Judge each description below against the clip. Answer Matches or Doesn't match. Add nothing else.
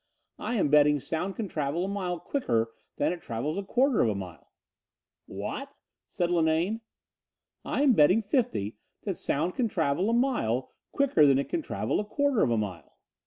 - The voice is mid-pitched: Matches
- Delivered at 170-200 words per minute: Matches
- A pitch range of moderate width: Doesn't match